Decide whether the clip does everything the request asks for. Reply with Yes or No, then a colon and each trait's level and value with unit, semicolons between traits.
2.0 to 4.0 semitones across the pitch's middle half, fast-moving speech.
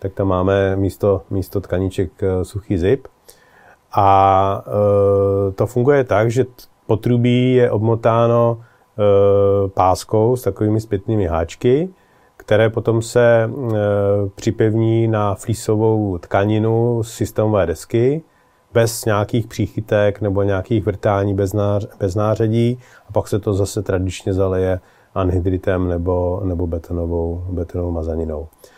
No: average, 2.8 semitones; average, 120 wpm